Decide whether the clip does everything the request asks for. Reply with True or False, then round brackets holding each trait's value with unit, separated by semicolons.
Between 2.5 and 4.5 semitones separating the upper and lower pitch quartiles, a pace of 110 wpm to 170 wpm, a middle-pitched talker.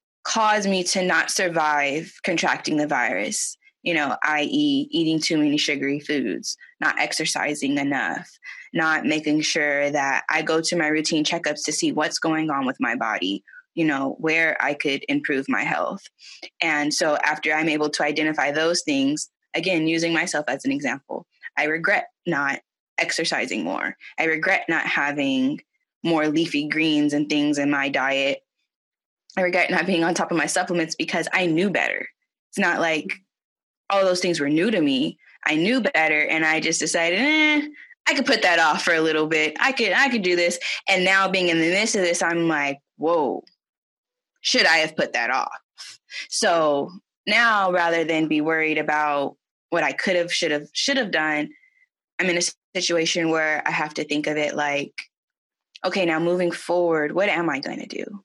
False (4.1 semitones; 185 wpm; 165 Hz)